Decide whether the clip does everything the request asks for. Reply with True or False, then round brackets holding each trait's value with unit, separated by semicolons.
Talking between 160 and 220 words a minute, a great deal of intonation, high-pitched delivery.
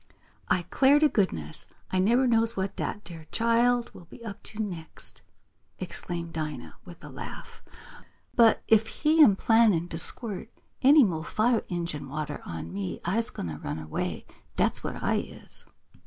True (165 wpm; 6.3 semitones; 195 Hz)